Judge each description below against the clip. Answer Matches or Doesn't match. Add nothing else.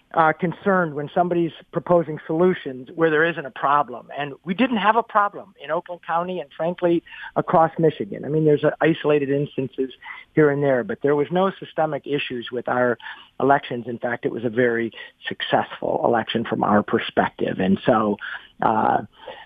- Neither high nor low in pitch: Matches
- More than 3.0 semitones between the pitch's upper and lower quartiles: Matches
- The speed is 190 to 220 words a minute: Doesn't match